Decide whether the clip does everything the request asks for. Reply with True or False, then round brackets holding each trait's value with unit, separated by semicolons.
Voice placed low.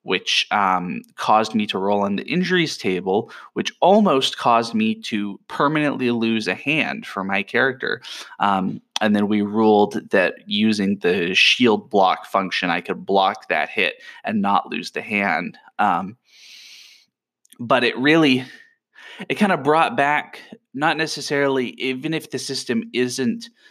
True (130 Hz)